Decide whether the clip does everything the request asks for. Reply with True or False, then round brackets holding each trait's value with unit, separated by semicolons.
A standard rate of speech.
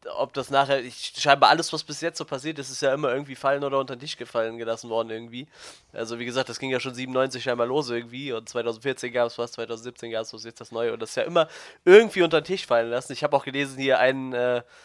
False (265 wpm)